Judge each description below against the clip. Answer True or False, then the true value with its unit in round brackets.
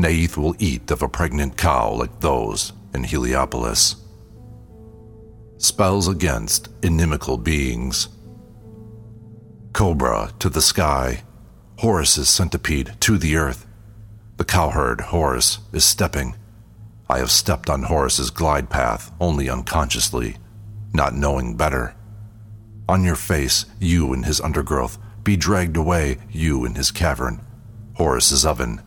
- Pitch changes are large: True (6.2 semitones)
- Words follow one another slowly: True (120 wpm)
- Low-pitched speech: True (90 Hz)